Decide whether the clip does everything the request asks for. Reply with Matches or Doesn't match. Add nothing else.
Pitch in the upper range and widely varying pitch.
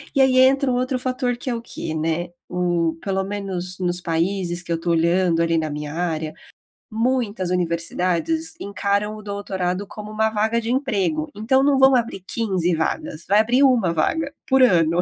Matches